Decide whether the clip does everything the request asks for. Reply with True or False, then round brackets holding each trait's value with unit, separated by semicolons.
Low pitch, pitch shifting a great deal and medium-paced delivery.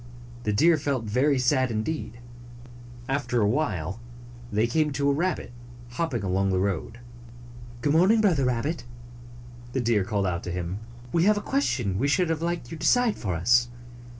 True (125 Hz; 6.9 semitones; 180 wpm)